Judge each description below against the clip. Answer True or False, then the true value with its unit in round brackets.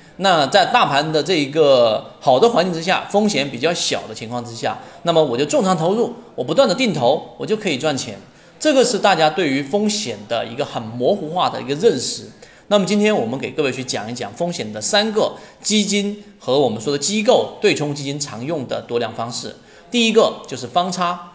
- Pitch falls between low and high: True (180 Hz)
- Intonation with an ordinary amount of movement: False (6.4 semitones)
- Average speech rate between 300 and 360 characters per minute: True (310 characters per minute)